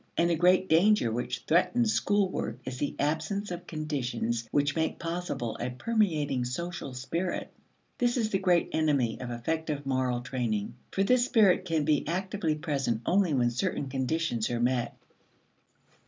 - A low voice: No, medium, 155 Hz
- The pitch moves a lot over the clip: Yes, wide, 6.3 semitones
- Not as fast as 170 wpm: Yes, average, 155 wpm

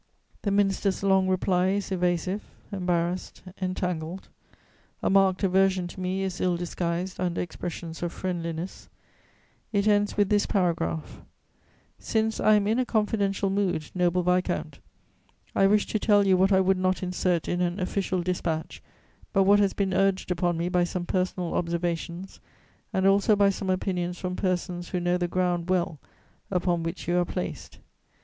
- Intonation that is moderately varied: No, narrow, 1.8 semitones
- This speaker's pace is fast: No, average, 160 wpm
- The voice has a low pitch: No, medium, 185 Hz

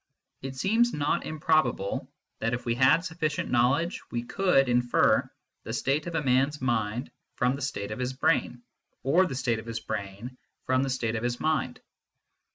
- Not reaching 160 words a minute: No, average, 185 wpm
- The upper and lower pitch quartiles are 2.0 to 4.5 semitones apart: Yes, average, 3.9 semitones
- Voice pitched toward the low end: Yes, low, 130 Hz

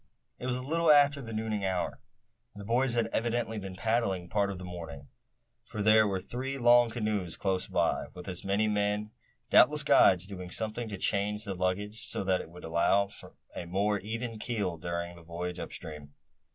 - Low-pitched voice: Yes, low, 100 Hz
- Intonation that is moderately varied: Yes, average, 3.8 semitones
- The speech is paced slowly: No, average, 190 wpm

